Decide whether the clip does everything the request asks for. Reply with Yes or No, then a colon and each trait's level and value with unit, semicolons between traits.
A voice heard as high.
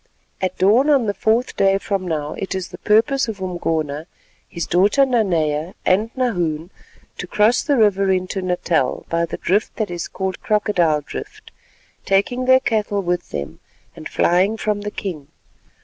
Yes: high, 195 Hz